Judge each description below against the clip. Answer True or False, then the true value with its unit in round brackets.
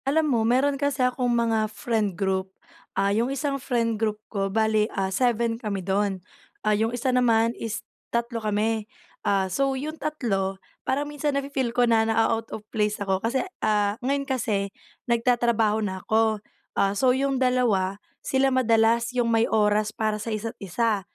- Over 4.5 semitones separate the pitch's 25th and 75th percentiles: False (3.2 semitones)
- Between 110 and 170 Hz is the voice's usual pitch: False (225 Hz)